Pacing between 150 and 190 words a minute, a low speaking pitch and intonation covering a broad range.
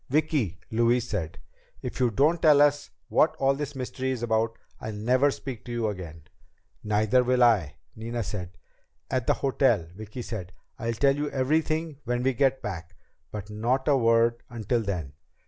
No: average, 170 wpm; low, 120 Hz; average, 4.1 semitones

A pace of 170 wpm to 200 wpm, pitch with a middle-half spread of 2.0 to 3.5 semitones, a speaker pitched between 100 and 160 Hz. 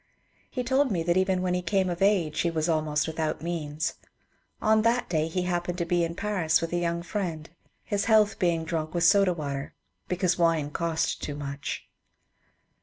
No: average, 185 wpm; average, 2.8 semitones; medium, 170 Hz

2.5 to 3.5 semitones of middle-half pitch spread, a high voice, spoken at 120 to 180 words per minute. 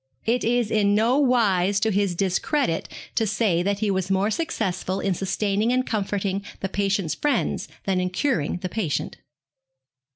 Yes: average, 3.0 semitones; high, 200 Hz; average, 160 wpm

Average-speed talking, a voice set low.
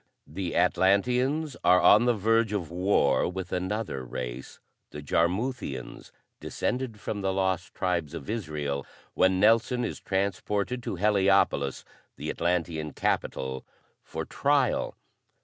No: slow, 120 wpm; very low, 95 Hz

